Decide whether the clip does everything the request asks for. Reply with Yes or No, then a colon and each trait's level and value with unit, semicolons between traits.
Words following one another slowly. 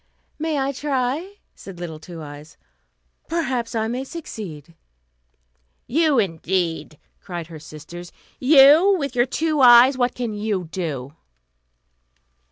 Yes: slow, 120 wpm